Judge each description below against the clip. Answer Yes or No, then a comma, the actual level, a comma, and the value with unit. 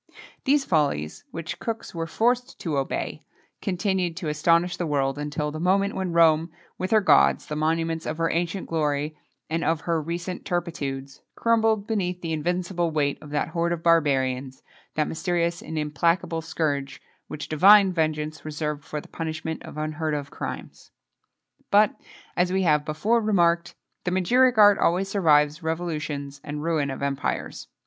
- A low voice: No, medium, 165 Hz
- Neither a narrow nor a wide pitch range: Yes, average, 3.1 semitones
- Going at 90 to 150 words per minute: No, average, 165 wpm